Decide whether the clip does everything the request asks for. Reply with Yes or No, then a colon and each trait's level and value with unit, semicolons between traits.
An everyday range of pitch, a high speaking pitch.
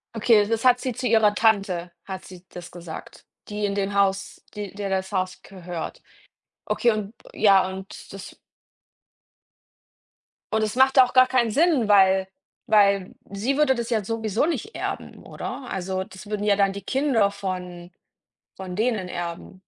Yes: average, 3.1 semitones; high, 200 Hz